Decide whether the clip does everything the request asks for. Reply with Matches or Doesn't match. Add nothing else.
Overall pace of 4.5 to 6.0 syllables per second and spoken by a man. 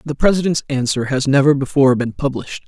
Doesn't match